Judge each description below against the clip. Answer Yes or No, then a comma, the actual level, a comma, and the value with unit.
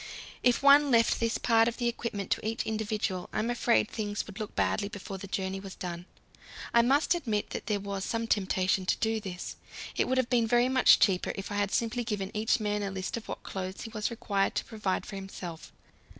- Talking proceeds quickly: Yes, fast, 220 wpm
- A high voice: Yes, high, 210 Hz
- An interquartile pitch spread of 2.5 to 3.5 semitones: Yes, average, 3.2 semitones